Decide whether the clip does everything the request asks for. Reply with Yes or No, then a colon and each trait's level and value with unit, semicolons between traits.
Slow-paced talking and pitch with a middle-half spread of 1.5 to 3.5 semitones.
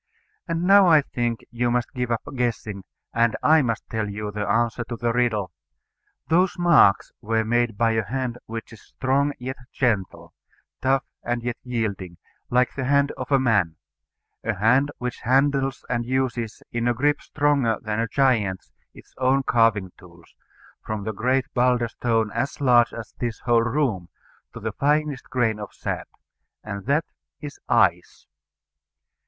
No: average, 165 wpm; average, 3.1 semitones